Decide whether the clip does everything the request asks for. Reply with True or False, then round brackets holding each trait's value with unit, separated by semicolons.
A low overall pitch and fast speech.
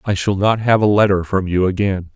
True (100 Hz; 250 wpm)